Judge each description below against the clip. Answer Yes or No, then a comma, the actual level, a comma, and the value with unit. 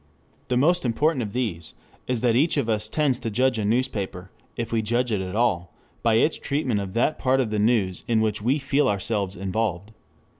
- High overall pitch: No, low, 115 Hz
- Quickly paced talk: Yes, fast, 210 wpm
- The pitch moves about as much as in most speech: Yes, average, 3.8 semitones